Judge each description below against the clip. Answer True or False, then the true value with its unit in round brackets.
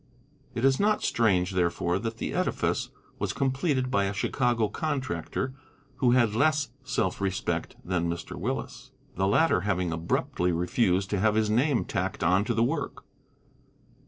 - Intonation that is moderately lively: False (6.0 semitones)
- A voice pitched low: True (110 Hz)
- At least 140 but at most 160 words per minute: True (155 wpm)